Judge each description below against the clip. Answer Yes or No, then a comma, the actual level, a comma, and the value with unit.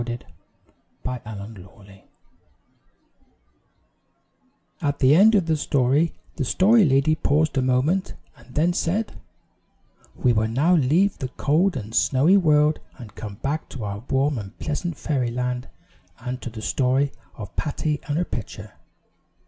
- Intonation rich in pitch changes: No, average, 4.8 semitones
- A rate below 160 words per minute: Yes, average, 145 wpm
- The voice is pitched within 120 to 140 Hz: Yes, low, 135 Hz